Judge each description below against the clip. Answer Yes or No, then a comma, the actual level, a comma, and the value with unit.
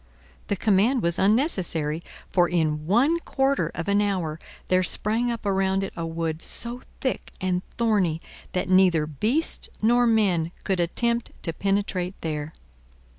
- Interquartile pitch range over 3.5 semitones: Yes, average, 5.1 semitones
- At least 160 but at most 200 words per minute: No, average, 145 wpm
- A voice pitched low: No, high, 190 Hz